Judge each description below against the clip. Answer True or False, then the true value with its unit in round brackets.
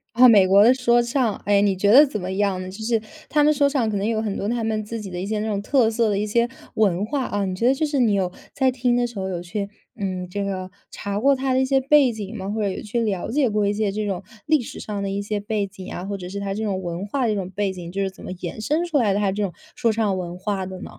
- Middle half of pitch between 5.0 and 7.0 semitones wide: False (3.5 semitones)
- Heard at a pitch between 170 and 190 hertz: False (210 Hz)